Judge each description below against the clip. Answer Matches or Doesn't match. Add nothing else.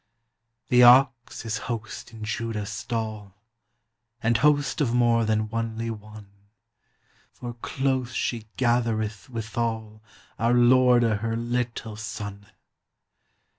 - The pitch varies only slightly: Matches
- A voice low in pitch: Matches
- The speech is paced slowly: Matches